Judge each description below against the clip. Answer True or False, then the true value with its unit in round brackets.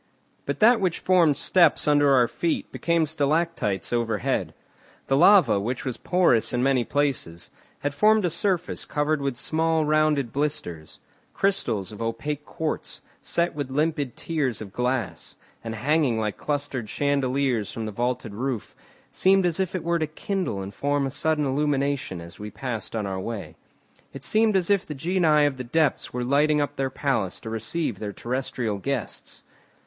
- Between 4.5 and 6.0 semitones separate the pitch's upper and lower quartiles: True (5.2 semitones)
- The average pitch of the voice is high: False (140 Hz)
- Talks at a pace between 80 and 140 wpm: False (165 wpm)